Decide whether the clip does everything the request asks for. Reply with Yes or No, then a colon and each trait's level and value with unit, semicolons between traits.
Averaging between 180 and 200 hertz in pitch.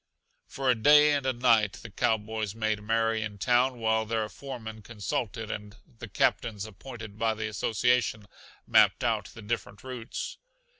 No: low, 110 Hz